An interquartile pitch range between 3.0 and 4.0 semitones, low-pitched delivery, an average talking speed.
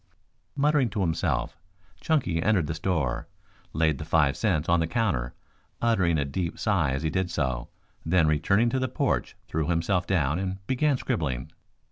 No: average, 5.2 semitones; very low, 85 Hz; average, 165 wpm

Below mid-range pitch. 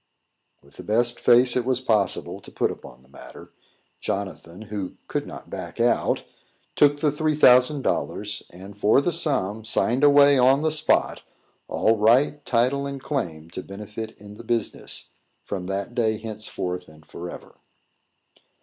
Yes: low, 115 Hz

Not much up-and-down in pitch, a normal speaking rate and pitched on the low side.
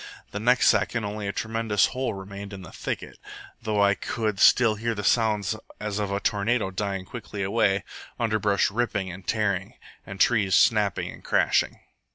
Yes: narrow, 2.2 semitones; average, 170 wpm; low, 105 Hz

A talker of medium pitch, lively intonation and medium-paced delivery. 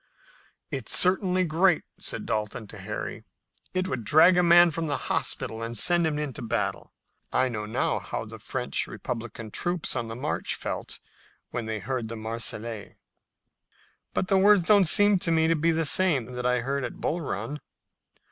Yes: medium, 145 Hz; wide, 7.1 semitones; average, 175 wpm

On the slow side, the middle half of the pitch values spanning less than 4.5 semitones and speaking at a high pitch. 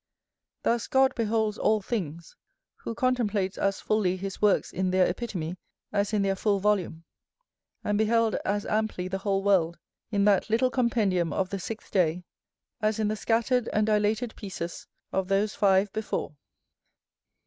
No: average, 155 wpm; narrow, 2.6 semitones; high, 205 Hz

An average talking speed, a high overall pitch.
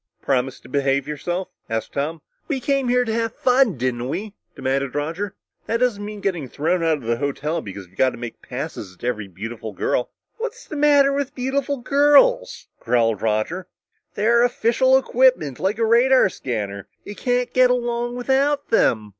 Yes: average, 175 wpm; high, 195 Hz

